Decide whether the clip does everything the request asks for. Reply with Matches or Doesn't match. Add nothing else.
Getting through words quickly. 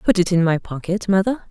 Matches